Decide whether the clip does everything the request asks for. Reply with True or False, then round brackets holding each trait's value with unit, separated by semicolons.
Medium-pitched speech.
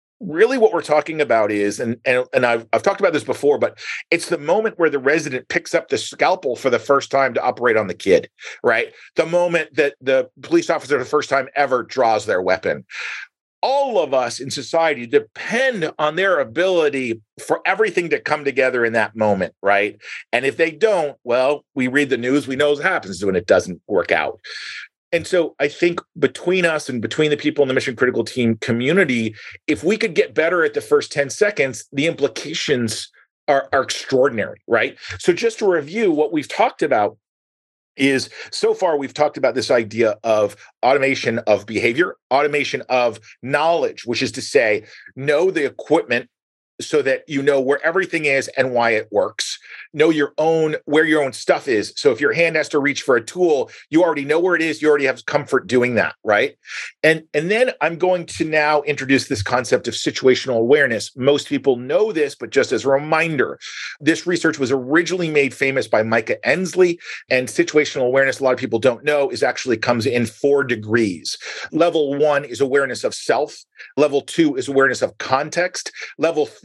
True (145 Hz)